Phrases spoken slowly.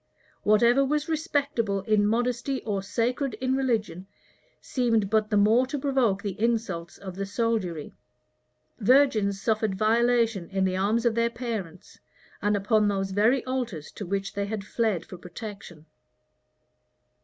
No: average, 145 wpm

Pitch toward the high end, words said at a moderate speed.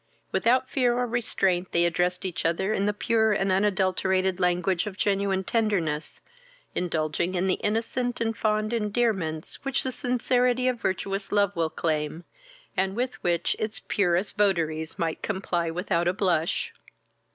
Yes: high, 195 Hz; average, 150 wpm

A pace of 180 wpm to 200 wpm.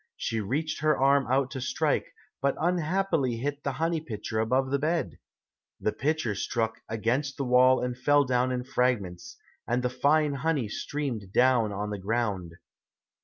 No: average, 165 wpm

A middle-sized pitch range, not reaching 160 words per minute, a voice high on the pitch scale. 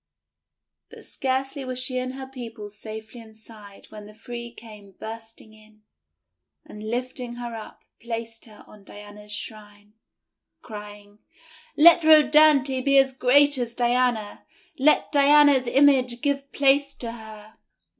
Yes: average, 3.8 semitones; slow, 135 wpm; high, 235 Hz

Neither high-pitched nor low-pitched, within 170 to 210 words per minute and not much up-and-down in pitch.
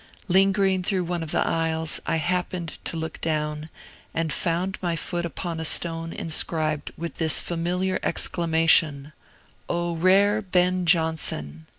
No: medium, 165 Hz; slow, 135 wpm; narrow, 2.0 semitones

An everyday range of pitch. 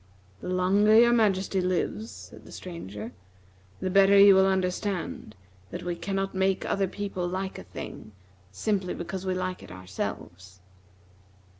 No: narrow, 1.9 semitones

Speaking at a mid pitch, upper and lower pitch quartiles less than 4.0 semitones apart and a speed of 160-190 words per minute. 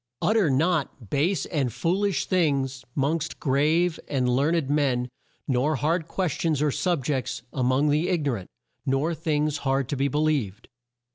Yes: medium, 145 Hz; average, 3.5 semitones; average, 180 wpm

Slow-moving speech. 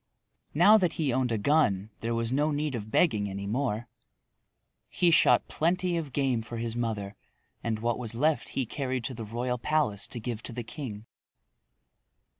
No: average, 180 wpm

